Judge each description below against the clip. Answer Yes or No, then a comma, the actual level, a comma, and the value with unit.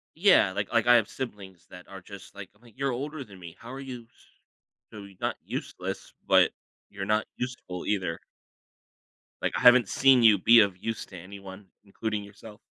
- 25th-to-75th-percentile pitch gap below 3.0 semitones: No, average, 3.9 semitones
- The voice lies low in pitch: Yes, low, 105 Hz